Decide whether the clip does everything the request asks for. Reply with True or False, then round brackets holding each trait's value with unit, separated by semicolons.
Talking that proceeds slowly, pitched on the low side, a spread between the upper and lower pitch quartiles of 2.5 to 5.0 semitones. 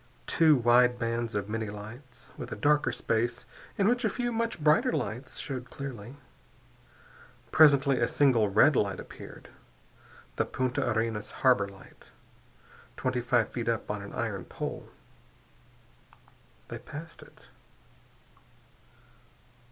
True (125 wpm; 125 Hz; 4.4 semitones)